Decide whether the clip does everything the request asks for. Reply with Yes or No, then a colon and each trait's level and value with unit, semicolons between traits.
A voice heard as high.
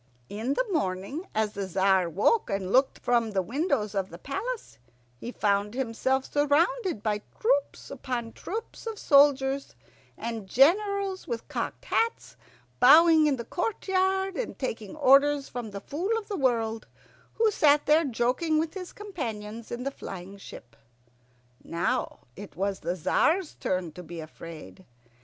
Yes: very high, 260 Hz